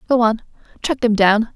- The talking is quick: No, average, 195 wpm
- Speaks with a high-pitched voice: Yes, high, 230 Hz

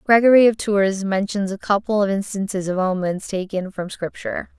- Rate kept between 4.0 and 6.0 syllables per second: Yes, 5.2 syllables/s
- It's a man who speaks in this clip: No, female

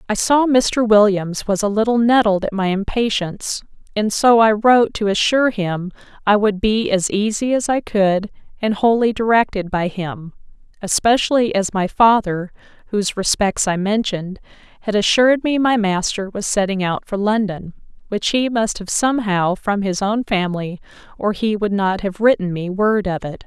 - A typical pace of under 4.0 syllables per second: No, 4.9 syllables/s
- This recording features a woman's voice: Yes, female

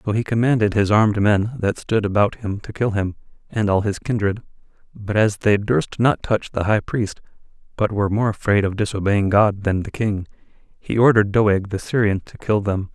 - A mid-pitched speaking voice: No, low, 105 Hz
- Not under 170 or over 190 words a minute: No, fast, 205 wpm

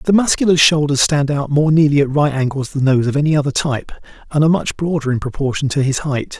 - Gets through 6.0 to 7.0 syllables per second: Yes, 6.3 syllables/s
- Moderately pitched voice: Yes, medium, 145 Hz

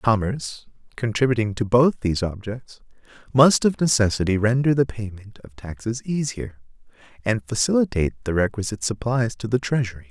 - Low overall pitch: Yes, low, 110 Hz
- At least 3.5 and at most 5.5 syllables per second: Yes, 5.4 syllables/s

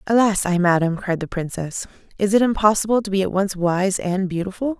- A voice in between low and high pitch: No, high, 195 Hz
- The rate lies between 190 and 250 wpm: Yes, average, 200 wpm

